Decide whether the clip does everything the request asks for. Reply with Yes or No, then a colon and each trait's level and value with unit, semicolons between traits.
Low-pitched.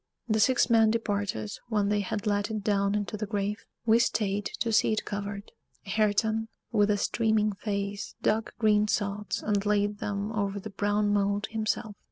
No: high, 210 Hz